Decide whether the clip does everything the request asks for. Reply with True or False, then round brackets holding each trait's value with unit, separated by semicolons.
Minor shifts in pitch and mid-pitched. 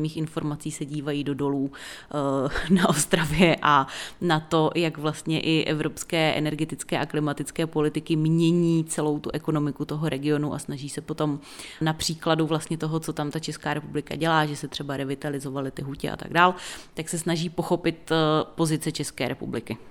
True (1.5 semitones; 155 Hz)